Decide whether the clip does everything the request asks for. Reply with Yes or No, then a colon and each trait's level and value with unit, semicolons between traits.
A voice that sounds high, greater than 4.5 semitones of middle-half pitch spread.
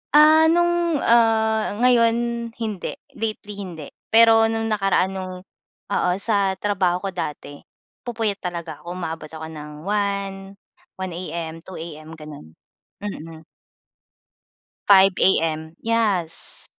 Yes: high, 195 Hz; average, 5.3 semitones